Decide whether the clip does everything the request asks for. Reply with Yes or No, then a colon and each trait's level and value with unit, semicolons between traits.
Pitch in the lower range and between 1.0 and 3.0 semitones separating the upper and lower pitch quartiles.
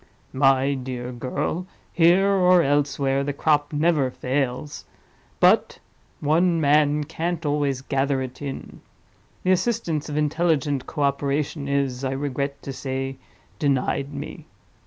No: medium, 145 Hz; narrow, 2.5 semitones